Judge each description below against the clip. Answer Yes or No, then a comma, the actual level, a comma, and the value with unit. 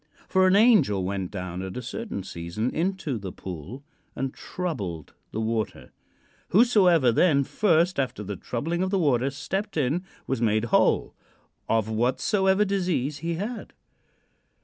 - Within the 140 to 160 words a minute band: Yes, average, 145 wpm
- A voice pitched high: No, low, 135 Hz